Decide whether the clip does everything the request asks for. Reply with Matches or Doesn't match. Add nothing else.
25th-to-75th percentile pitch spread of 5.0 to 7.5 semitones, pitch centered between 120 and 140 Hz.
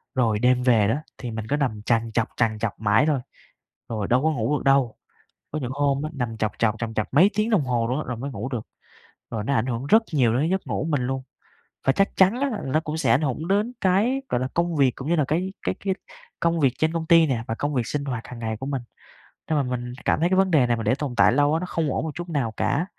Matches